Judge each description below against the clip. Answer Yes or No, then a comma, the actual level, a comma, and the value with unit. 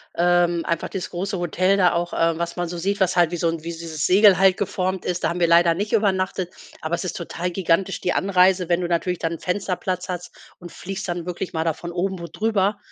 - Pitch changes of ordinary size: No, narrow, 1.8 semitones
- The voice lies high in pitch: No, medium, 180 Hz